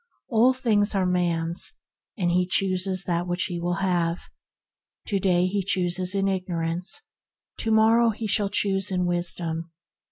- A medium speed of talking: Yes, average, 155 wpm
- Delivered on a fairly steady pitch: Yes, narrow, 2.2 semitones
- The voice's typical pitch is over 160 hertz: Yes, medium, 185 Hz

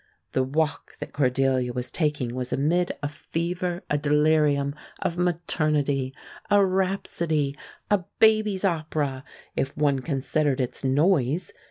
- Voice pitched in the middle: Yes, medium, 150 Hz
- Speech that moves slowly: Yes, slow, 125 wpm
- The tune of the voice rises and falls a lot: No, average, 4.2 semitones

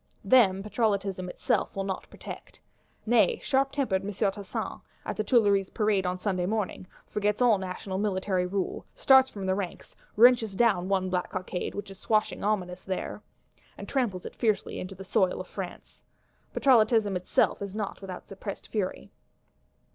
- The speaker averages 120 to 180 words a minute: Yes, average, 160 wpm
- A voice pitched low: No, high, 200 Hz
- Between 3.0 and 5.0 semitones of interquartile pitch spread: No, narrow, 2.5 semitones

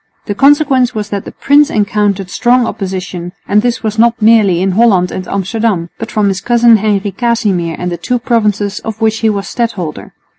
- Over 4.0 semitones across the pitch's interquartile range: No, average, 3.4 semitones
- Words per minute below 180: No, average, 185 wpm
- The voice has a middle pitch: No, high, 210 Hz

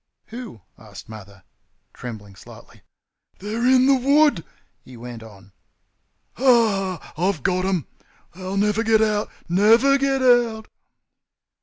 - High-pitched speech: Yes, high, 205 Hz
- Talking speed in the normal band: No, slow, 125 wpm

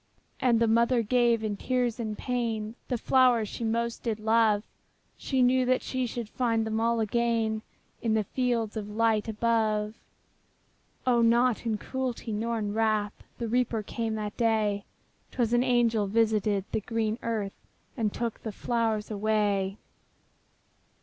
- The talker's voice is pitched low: No, high, 225 Hz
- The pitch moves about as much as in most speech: No, narrow, 1.8 semitones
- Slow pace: No, average, 150 wpm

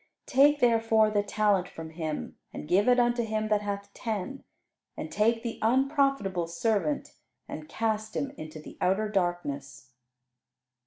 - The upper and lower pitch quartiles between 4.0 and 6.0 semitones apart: Yes, average, 4.6 semitones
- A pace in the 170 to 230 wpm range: No, average, 145 wpm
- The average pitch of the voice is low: No, high, 210 Hz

